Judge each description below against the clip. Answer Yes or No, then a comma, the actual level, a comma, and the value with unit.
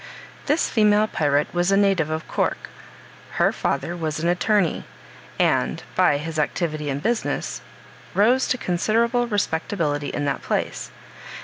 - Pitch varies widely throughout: Yes, wide, 5.8 semitones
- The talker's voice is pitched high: No, medium, 175 Hz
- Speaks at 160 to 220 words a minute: No, slow, 135 wpm